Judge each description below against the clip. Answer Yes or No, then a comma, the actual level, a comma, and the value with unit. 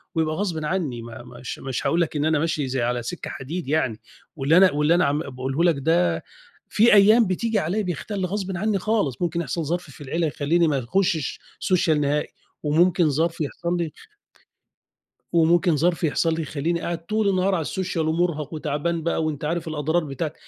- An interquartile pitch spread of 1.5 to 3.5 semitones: Yes, average, 3.2 semitones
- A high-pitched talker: No, medium, 160 Hz